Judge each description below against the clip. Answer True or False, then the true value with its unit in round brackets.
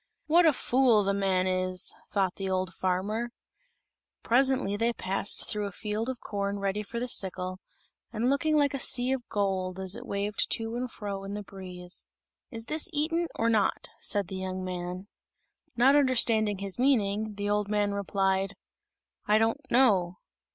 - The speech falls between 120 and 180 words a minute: True (170 wpm)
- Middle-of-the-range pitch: False (205 Hz)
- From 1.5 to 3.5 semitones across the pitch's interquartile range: False (3.9 semitones)